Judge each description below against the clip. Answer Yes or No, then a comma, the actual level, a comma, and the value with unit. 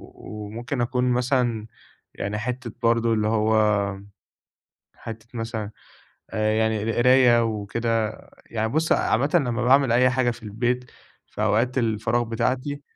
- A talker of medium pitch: No, low, 115 Hz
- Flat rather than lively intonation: Yes, narrow, 2.3 semitones